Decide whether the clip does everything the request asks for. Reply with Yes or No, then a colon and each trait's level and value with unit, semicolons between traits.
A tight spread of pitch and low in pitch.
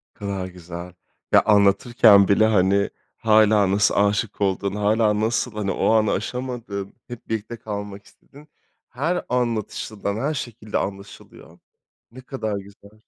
Yes: narrow, 2.3 semitones; low, 105 Hz